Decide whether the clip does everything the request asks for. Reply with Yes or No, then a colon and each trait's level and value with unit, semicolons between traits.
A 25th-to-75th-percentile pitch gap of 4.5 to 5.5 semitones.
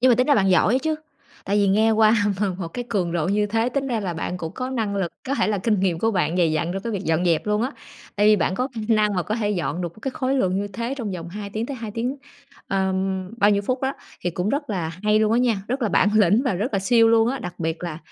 No: average, 4.1 semitones